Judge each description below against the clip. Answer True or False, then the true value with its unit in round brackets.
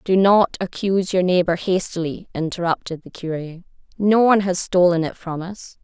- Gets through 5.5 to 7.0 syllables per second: False (4.9 syllables/s)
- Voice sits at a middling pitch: True (180 Hz)